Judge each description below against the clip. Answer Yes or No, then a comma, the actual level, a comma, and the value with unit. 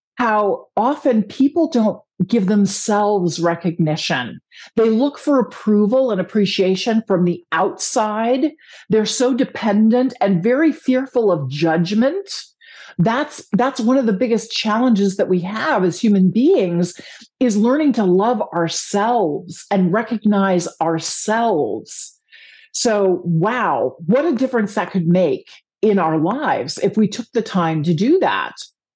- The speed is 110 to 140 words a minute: Yes, slow, 135 wpm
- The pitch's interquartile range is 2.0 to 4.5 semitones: No, wide, 5.5 semitones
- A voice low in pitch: No, high, 215 Hz